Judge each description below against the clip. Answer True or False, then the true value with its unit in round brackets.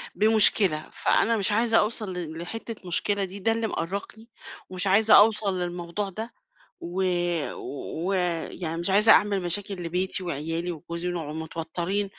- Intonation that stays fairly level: False (3.4 semitones)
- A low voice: False (185 Hz)